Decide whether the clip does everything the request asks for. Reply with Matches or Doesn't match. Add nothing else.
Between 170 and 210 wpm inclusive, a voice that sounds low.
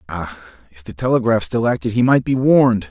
Matches